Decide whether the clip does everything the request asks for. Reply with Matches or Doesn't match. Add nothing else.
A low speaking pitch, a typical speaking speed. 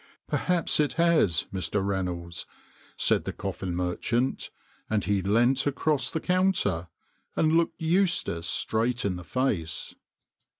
Doesn't match